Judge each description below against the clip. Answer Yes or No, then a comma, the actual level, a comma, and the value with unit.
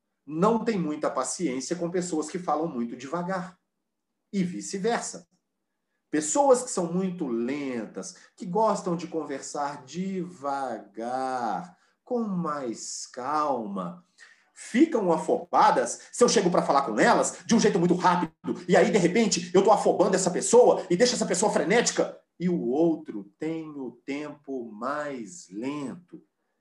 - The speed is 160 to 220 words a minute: No, average, 140 wpm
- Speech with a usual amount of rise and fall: No, wide, 6.3 semitones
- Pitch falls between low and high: Yes, medium, 175 Hz